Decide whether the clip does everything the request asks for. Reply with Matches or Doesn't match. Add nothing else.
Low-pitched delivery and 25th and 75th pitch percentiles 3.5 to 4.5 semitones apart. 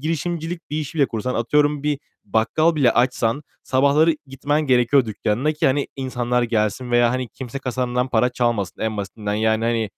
Matches